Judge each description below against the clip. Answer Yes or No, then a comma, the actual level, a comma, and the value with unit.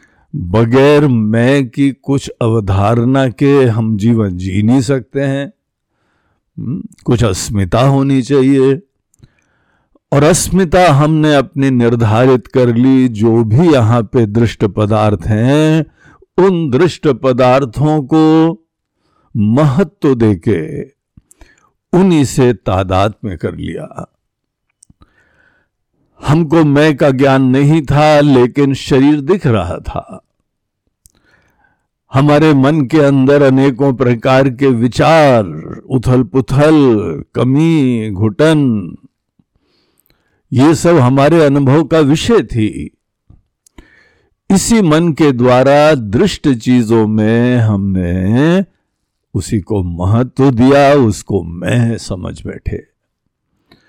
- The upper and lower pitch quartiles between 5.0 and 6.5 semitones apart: No, average, 4.3 semitones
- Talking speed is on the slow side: Yes, slow, 100 wpm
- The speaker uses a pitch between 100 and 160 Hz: Yes, low, 135 Hz